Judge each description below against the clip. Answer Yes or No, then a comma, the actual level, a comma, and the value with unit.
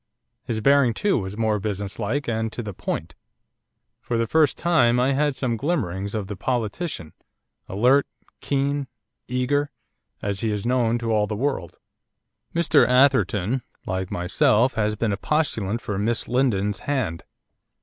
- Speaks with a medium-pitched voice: No, low, 115 Hz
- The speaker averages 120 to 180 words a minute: Yes, average, 150 wpm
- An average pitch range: Yes, average, 4.7 semitones